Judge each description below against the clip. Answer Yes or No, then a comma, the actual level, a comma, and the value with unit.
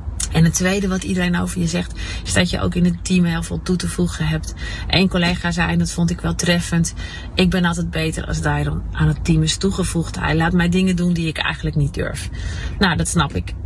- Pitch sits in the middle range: Yes, medium, 165 Hz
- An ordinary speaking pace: No, fast, 240 wpm